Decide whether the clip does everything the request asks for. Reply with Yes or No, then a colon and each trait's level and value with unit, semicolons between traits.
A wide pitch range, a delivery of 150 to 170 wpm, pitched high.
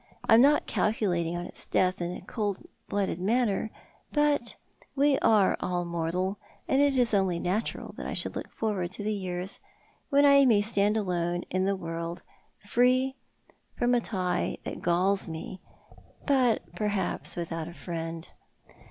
No: average, 4.9 semitones; average, 160 wpm; high, 195 Hz